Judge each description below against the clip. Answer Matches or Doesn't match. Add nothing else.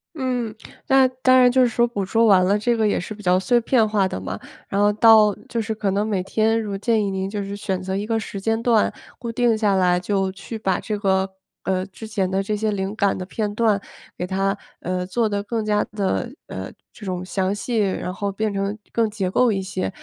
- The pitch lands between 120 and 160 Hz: Doesn't match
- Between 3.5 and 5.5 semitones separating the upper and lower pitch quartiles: Doesn't match